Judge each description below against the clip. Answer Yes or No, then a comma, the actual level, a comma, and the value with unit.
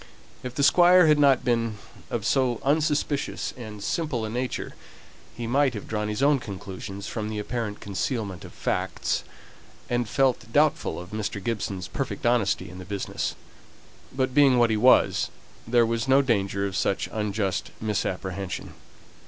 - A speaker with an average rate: Yes, average, 155 wpm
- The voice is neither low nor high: No, low, 115 Hz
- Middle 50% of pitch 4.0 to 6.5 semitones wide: Yes, average, 4.4 semitones